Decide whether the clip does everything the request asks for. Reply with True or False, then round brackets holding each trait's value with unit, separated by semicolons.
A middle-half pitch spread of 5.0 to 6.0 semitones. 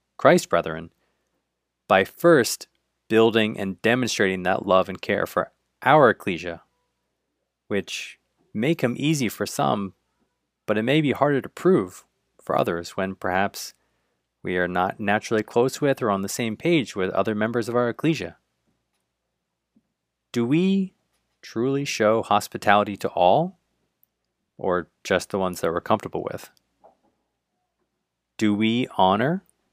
True (5.3 semitones)